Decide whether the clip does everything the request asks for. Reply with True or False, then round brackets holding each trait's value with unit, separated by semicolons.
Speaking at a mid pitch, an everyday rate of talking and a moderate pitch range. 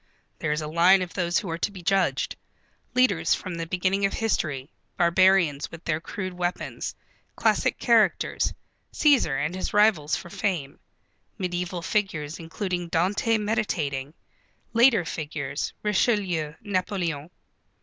False (175 Hz; 130 wpm; 3.6 semitones)